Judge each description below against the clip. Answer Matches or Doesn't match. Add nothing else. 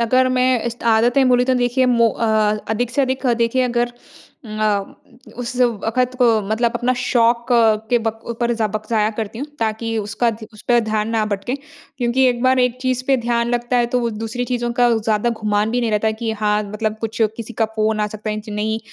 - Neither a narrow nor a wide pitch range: Doesn't match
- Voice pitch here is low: Doesn't match